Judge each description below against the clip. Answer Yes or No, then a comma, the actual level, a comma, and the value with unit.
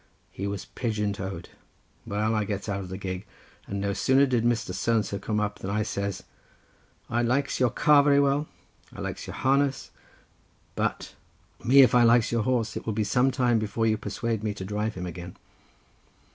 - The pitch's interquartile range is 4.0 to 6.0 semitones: No, average, 3.6 semitones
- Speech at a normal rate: No, fast, 210 wpm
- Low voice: Yes, low, 110 Hz